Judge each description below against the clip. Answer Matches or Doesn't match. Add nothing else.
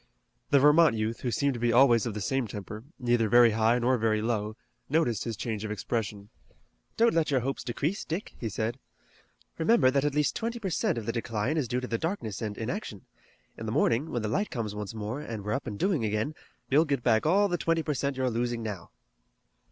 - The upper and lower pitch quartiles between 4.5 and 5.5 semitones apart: Matches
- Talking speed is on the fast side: Matches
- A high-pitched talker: Doesn't match